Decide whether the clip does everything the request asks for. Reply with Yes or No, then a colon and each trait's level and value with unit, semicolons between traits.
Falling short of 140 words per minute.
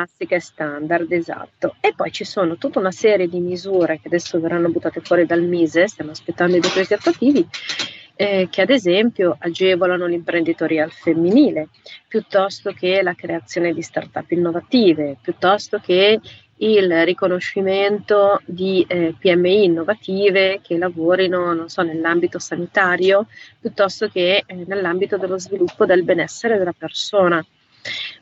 Yes: average, 130 wpm